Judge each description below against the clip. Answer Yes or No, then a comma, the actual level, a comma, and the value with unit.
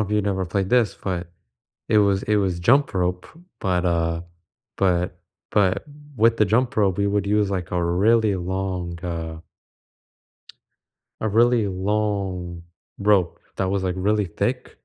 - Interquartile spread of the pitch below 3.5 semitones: Yes, average, 2.8 semitones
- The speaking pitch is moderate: No, very low, 95 Hz